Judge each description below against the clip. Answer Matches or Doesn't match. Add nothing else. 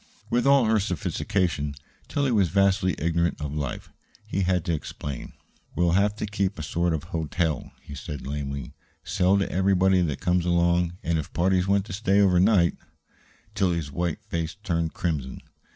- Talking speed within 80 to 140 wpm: Doesn't match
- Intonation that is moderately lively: Matches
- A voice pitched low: Matches